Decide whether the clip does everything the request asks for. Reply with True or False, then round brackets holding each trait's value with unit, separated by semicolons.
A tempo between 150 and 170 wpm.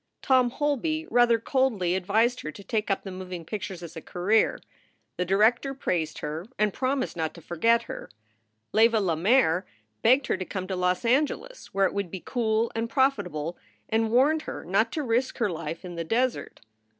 False (185 wpm)